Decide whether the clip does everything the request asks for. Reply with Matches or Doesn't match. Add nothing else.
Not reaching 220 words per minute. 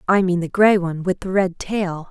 Doesn't match